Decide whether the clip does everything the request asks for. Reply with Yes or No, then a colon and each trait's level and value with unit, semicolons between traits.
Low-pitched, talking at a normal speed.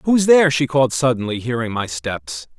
Yes: low, 125 Hz; average, 185 wpm